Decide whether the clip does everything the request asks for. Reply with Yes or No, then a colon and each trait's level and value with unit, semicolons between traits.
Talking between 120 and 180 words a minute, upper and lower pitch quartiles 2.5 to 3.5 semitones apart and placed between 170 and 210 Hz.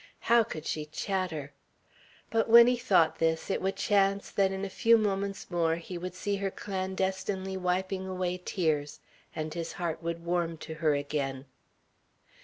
Yes: average, 165 wpm; average, 3.1 semitones; medium, 185 Hz